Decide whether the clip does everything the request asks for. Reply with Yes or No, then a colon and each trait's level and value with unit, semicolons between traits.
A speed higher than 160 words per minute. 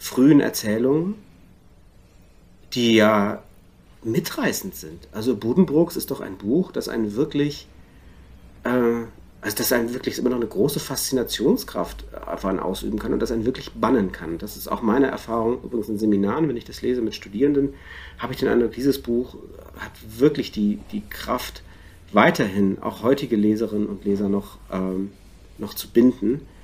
No: average, 155 wpm